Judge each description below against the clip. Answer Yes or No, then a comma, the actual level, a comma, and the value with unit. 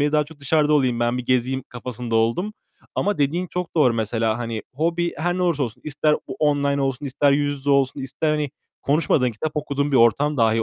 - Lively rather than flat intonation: No, average, 3.5 semitones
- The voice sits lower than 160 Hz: Yes, medium, 140 Hz